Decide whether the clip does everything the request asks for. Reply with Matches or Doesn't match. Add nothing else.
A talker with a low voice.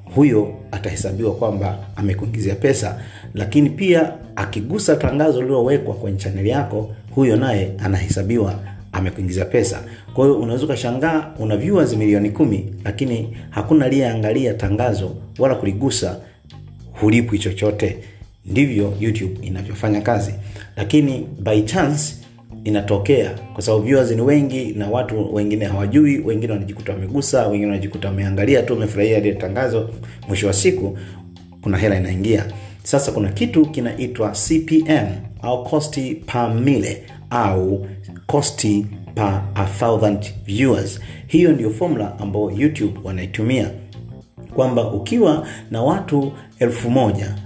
Matches